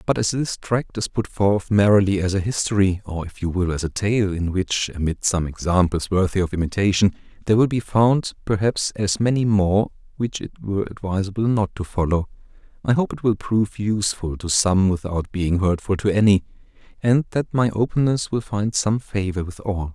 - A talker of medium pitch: No, low, 100 Hz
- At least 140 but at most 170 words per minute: No, average, 195 wpm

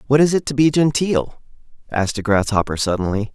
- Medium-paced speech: Yes, average, 180 wpm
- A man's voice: Yes, male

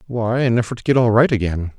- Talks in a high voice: No, low, 115 Hz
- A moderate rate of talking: No, fast, 270 wpm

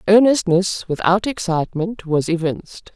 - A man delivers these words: No, female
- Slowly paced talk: Yes, slow, 100 wpm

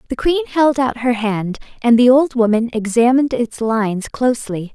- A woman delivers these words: Yes, female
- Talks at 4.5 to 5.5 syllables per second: Yes, 5.0 syllables/s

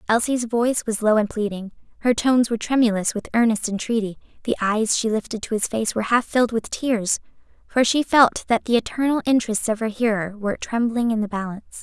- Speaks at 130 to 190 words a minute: No, fast, 205 wpm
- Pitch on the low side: No, high, 225 Hz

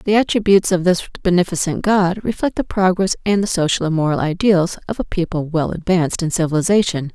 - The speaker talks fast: No, average, 185 wpm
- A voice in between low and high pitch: Yes, medium, 180 Hz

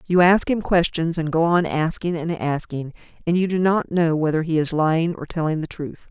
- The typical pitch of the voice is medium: Yes, medium, 165 Hz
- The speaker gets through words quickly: Yes, fast, 225 wpm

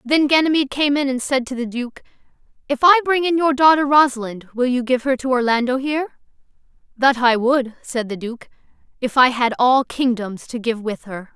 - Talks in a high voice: Yes, very high, 260 Hz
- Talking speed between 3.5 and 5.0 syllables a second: No, 5.3 syllables/s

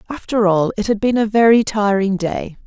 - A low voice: No, high, 210 Hz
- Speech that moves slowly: No, average, 200 wpm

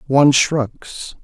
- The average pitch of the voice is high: No, low, 135 Hz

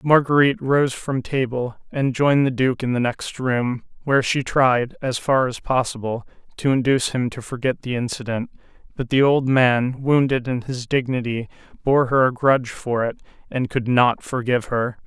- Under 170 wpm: No, average, 180 wpm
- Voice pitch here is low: Yes, low, 130 Hz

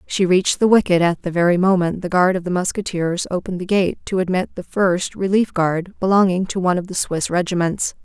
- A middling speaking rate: No, fast, 215 wpm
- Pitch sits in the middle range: Yes, medium, 180 Hz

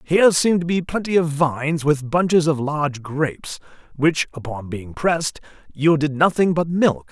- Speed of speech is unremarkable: Yes, average, 170 wpm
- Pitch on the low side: No, medium, 150 Hz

